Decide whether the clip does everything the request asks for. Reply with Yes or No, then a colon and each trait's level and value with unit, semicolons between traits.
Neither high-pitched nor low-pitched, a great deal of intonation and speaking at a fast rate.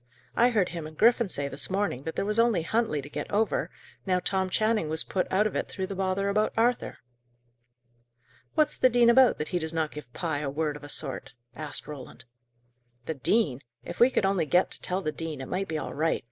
Yes: medium, 180 Hz; wide, 5.7 semitones; fast, 230 wpm